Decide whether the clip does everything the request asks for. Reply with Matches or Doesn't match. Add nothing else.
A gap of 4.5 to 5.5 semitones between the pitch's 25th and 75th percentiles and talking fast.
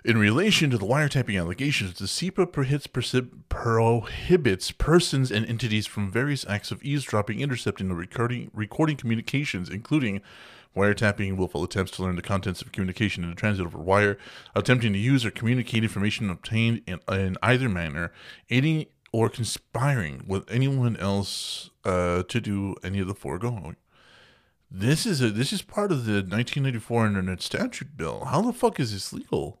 Doesn't match